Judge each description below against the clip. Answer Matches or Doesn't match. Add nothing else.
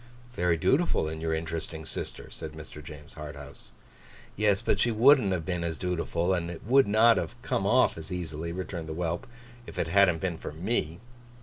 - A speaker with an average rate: Matches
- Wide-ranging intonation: Doesn't match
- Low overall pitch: Matches